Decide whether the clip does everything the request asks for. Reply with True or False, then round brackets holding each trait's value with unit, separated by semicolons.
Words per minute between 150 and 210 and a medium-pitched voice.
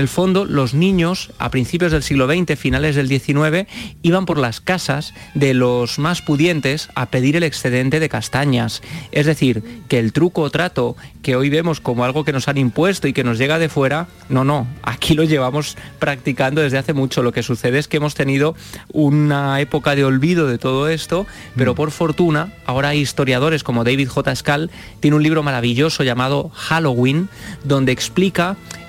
True (185 wpm; 145 Hz)